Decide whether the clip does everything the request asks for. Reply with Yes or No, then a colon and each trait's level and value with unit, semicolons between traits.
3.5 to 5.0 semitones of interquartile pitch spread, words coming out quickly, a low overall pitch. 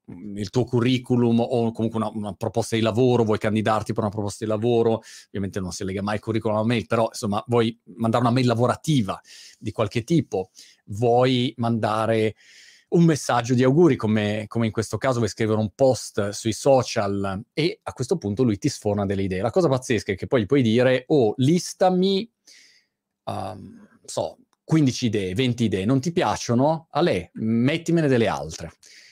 No: average, 3.0 semitones; fast, 180 wpm; low, 115 Hz